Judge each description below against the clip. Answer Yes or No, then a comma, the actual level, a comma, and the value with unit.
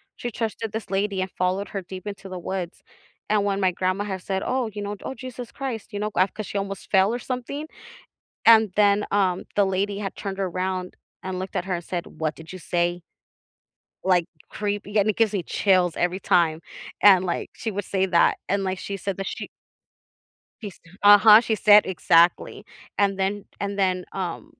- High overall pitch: Yes, high, 195 Hz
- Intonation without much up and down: Yes, narrow, 2.0 semitones